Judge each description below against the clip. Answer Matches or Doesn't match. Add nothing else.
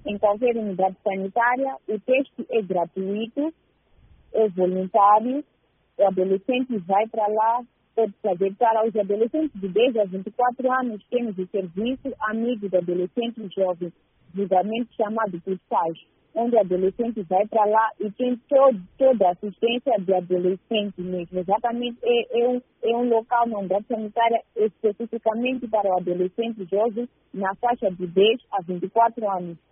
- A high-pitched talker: Matches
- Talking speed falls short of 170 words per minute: Matches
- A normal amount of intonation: Matches